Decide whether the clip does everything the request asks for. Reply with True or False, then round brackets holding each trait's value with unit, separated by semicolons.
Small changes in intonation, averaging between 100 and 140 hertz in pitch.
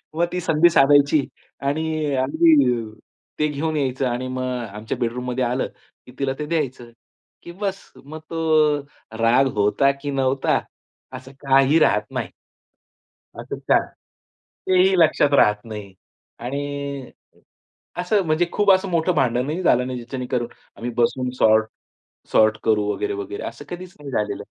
False (4.4 semitones; 135 Hz)